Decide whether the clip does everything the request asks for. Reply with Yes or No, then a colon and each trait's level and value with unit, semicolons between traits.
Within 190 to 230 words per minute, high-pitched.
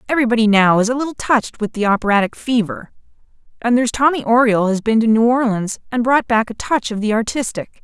Yes: fast, 205 wpm; high, 230 Hz